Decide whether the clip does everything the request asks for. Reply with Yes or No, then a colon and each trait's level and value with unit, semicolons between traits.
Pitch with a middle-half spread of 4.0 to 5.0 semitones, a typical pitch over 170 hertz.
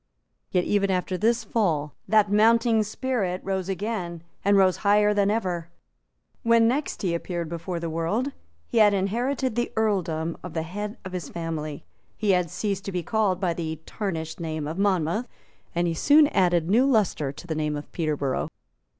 Yes: average, 4.3 semitones; medium, 185 Hz